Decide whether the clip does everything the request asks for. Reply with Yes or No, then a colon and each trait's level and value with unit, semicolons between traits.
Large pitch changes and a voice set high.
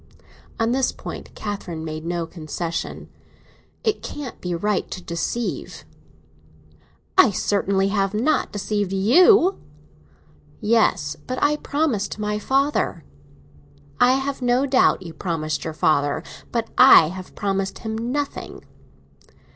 Yes: wide, 6.6 semitones; high, 210 Hz